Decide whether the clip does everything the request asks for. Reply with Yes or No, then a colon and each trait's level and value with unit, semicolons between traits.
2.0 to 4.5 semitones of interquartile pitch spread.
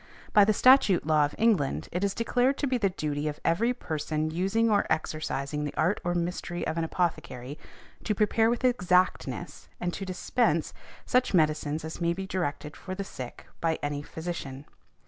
No: average, 4.9 semitones